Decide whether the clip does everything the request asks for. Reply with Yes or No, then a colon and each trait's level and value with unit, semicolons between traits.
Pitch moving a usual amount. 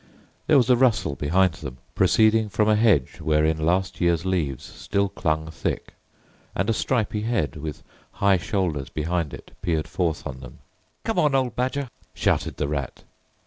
No: wide, 6.0 semitones